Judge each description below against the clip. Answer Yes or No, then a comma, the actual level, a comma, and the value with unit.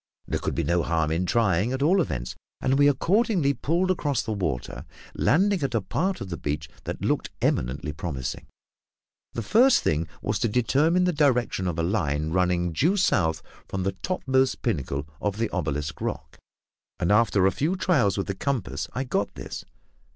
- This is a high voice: No, low, 105 Hz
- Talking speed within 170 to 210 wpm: Yes, average, 180 wpm